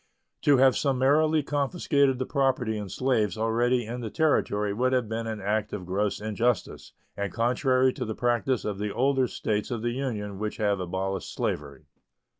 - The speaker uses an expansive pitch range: No, average, 4.0 semitones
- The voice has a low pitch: Yes, low, 115 Hz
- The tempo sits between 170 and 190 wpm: Yes, average, 175 wpm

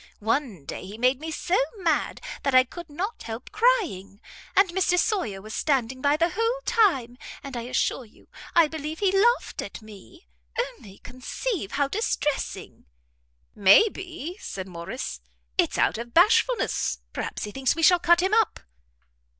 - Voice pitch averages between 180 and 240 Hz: No, very high, 300 Hz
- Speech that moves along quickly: No, average, 160 wpm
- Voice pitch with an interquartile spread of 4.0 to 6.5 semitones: No, wide, 8.3 semitones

